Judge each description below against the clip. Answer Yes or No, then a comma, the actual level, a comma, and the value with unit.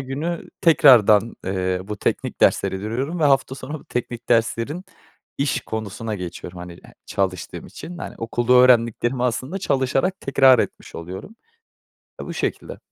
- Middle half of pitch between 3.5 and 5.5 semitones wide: Yes, average, 4.6 semitones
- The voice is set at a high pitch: No, low, 120 Hz